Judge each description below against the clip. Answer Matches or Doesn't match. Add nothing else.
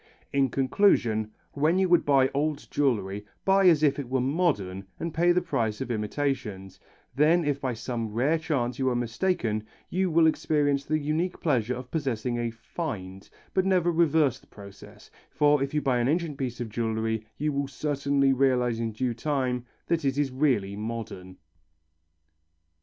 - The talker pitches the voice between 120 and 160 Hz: Matches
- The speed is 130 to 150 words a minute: Doesn't match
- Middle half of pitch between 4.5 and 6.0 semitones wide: Matches